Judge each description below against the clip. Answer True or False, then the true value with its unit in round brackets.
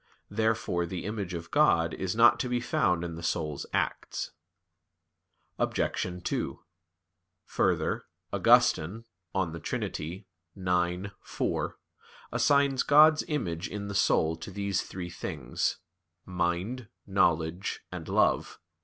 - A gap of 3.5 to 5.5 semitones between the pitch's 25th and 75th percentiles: True (4.4 semitones)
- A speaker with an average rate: False (115 wpm)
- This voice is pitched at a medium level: False (90 Hz)